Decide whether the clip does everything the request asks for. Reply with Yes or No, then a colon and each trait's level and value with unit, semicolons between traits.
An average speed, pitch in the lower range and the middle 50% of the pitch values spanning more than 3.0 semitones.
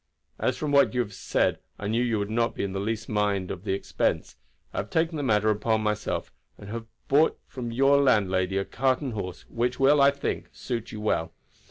No: fast, 215 wpm; low, 115 Hz; average, 4.4 semitones